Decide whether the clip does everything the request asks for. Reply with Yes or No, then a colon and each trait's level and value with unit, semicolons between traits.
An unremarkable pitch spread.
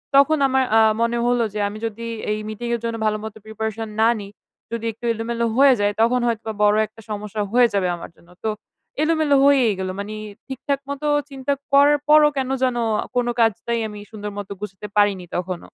Yes: average, 3.9 semitones